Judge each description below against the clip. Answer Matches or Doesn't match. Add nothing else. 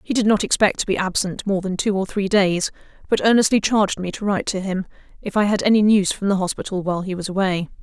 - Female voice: Matches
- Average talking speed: Doesn't match